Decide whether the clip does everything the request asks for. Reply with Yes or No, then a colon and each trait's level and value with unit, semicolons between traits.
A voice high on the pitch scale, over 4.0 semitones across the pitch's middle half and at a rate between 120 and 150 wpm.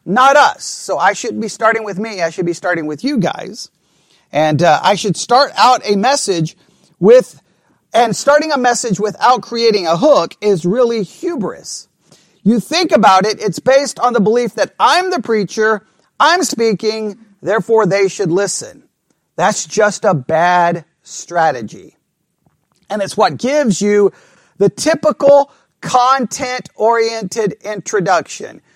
Yes: high, 215 Hz; average, 4.7 semitones; average, 145 wpm